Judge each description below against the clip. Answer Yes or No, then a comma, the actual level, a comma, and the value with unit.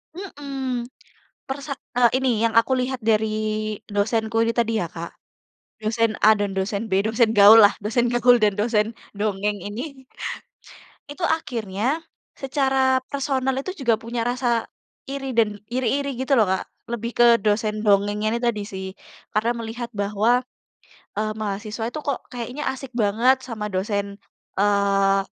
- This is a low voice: No, high, 230 Hz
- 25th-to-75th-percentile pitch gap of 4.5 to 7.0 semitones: No, average, 3.7 semitones